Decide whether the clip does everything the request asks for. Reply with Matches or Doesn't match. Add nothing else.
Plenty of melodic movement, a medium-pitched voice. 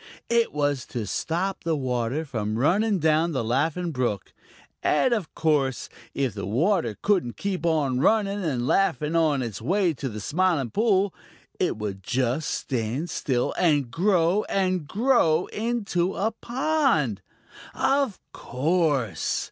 Matches